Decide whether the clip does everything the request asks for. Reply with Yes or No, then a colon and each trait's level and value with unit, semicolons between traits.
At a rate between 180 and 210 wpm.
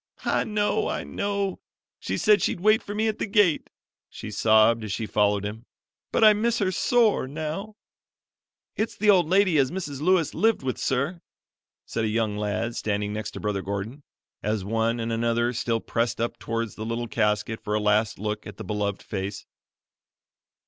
Yes: average, 185 wpm